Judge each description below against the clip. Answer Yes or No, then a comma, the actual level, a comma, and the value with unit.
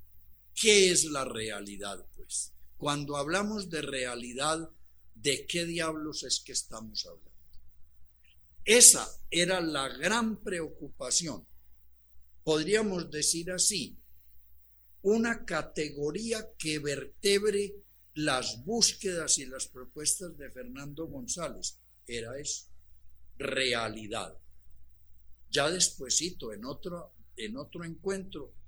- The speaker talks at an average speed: No, slow, 95 wpm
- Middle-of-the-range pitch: Yes, medium, 145 Hz